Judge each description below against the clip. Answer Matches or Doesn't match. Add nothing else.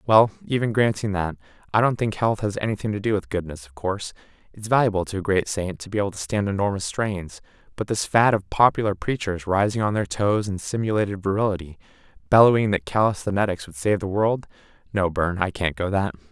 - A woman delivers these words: Doesn't match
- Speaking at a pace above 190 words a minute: Matches